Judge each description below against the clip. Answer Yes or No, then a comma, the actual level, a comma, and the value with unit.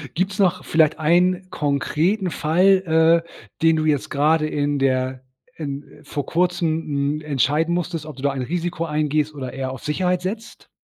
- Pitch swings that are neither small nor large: Yes, average, 3.4 semitones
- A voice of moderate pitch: Yes, medium, 155 Hz